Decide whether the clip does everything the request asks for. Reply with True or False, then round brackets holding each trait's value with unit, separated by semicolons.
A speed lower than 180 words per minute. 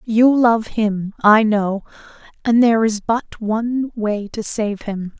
True (160 wpm)